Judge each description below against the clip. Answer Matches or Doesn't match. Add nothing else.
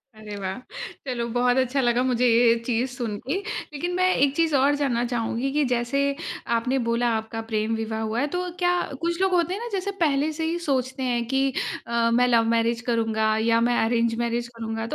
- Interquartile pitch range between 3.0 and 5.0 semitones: Matches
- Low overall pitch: Doesn't match